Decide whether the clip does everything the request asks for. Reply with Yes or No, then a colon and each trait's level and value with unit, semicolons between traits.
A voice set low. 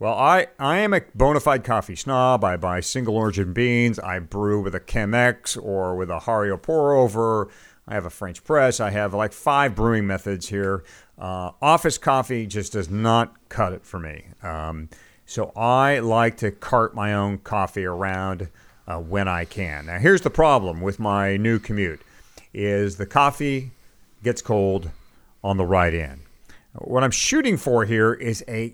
Yes: low, 105 Hz